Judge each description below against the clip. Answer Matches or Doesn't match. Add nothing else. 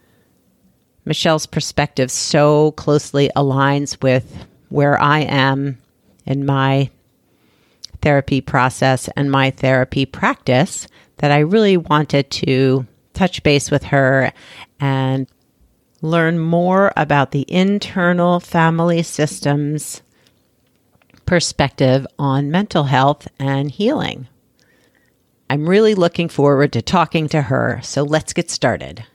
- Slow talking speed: Matches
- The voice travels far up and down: Doesn't match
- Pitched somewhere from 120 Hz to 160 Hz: Matches